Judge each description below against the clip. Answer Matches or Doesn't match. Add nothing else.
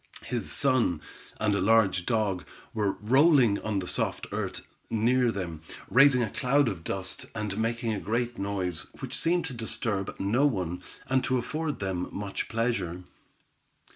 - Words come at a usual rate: Matches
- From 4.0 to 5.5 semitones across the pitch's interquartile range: Matches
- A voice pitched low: Matches